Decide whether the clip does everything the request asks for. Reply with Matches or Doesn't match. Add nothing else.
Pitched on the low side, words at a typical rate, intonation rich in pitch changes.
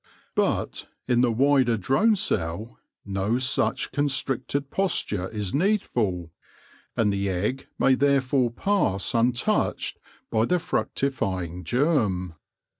Doesn't match